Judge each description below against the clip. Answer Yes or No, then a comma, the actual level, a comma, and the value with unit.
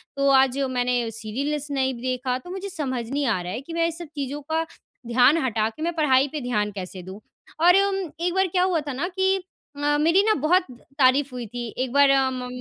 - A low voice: No, very high, 275 Hz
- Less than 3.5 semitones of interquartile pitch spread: No, average, 5.1 semitones